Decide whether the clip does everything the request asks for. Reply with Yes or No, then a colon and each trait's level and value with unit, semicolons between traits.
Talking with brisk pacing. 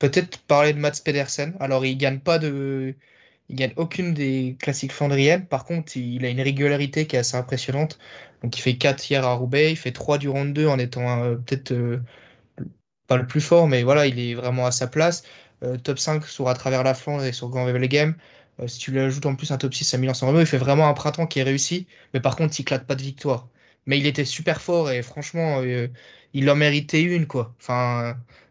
Yes: fast, 240 wpm